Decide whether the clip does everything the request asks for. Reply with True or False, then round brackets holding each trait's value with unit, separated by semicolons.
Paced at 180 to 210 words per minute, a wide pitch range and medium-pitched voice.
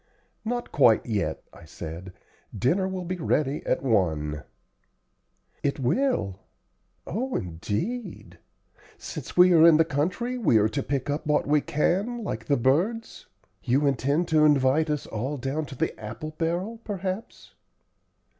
False (145 wpm; 7.1 semitones; 150 Hz)